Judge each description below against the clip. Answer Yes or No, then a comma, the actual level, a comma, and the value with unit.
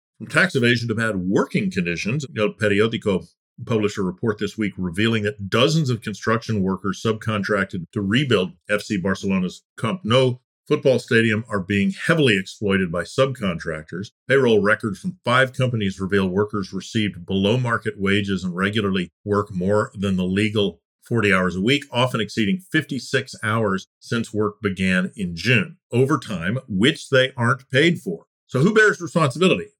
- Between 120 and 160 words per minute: Yes, average, 150 wpm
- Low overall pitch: Yes, low, 110 Hz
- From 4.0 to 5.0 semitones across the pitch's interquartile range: Yes, average, 4.7 semitones